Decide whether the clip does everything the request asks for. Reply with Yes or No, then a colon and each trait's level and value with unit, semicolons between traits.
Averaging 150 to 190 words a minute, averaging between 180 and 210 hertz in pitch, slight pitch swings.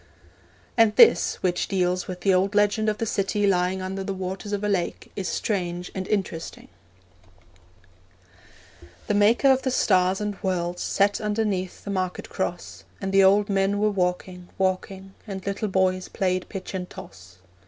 Yes: average, 165 wpm; high, 190 Hz; narrow, 2.0 semitones